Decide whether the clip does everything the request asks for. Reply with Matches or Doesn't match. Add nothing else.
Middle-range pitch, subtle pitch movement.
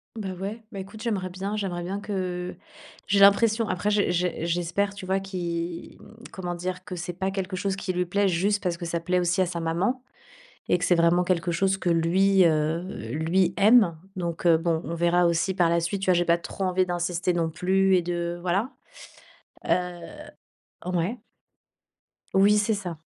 Matches